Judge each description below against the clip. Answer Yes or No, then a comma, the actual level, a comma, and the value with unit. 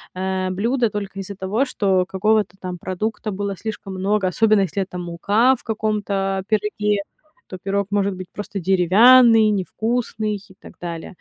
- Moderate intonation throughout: No, narrow, 2.3 semitones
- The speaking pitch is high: Yes, high, 200 Hz